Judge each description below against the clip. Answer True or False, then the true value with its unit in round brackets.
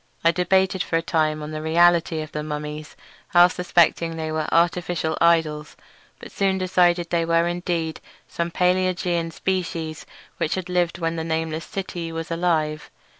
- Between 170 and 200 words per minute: False (160 wpm)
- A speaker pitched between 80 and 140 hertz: False (165 Hz)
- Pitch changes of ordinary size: False (1.9 semitones)